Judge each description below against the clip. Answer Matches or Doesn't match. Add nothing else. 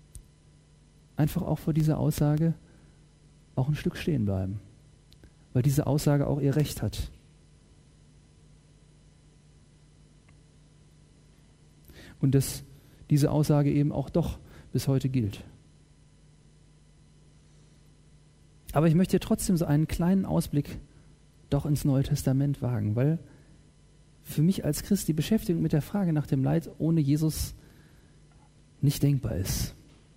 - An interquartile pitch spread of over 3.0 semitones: Doesn't match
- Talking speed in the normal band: Doesn't match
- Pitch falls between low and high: Matches